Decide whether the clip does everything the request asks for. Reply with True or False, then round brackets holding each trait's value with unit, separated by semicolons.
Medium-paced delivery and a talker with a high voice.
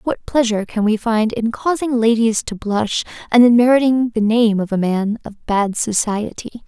True (190 wpm; 225 Hz)